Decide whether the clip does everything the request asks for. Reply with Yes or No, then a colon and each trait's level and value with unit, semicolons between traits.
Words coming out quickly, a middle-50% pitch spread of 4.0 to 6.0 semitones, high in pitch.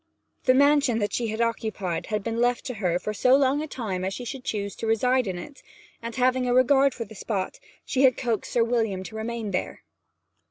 No: fast, 215 wpm; average, 3.4 semitones; high, 230 Hz